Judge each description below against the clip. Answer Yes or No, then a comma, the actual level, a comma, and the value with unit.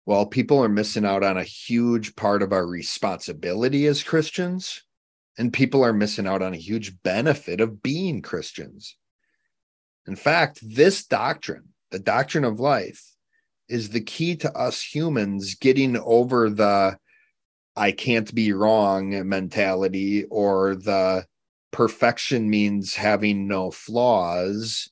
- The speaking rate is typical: No, slow, 130 wpm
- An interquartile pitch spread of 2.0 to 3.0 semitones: No, average, 4.4 semitones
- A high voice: No, low, 105 Hz